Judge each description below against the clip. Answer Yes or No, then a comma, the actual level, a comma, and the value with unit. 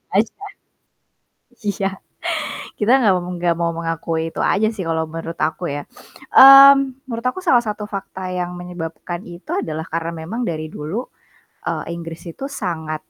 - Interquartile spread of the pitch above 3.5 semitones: Yes, average, 4.9 semitones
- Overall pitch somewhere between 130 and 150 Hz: No, medium, 175 Hz